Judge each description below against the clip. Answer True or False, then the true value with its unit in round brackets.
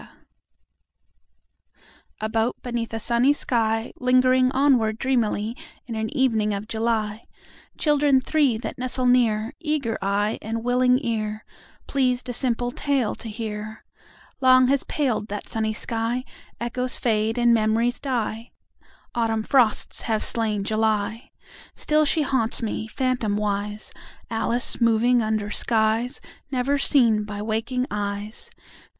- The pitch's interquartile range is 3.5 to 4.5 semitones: False (2.7 semitones)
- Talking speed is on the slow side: True (125 wpm)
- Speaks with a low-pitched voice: False (230 Hz)